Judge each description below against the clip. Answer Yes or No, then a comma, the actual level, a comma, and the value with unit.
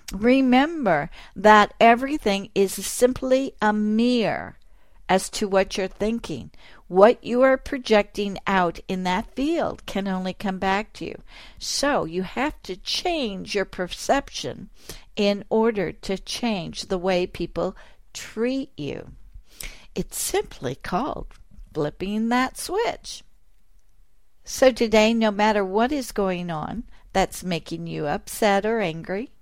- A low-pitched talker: No, high, 210 Hz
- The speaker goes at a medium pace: No, slow, 125 wpm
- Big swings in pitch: No, average, 4.3 semitones